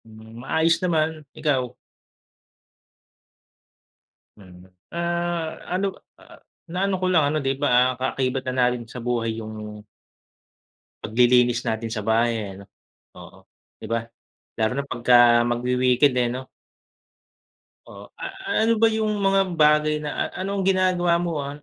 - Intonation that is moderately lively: No, wide, 6.4 semitones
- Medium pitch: No, low, 130 Hz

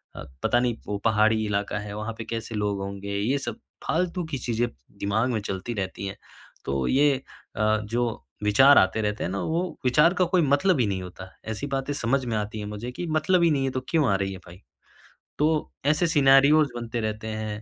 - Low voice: Yes, low, 115 Hz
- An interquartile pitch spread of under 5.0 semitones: No, wide, 5.4 semitones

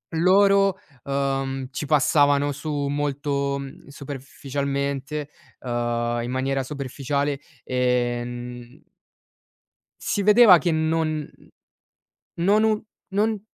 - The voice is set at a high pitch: No, medium, 140 Hz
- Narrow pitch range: No, average, 3.3 semitones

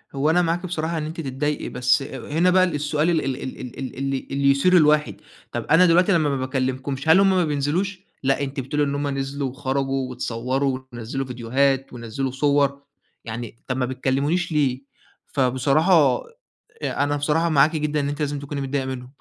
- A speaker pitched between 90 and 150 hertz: Yes, medium, 140 Hz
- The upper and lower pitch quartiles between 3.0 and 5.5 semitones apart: No, narrow, 2.6 semitones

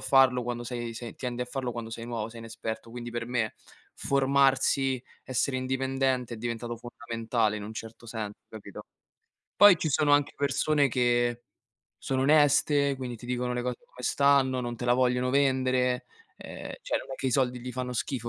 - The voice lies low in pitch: Yes, low, 125 Hz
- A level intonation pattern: Yes, narrow, 2.0 semitones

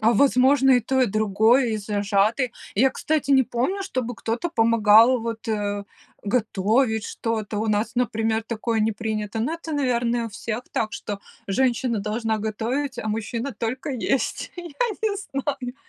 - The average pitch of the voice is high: Yes, high, 230 Hz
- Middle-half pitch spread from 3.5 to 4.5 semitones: No, average, 3.1 semitones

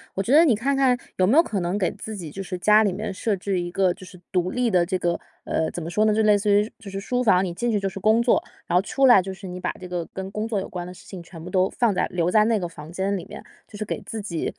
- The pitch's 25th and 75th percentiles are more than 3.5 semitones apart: No, average, 3.1 semitones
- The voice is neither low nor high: No, high, 195 Hz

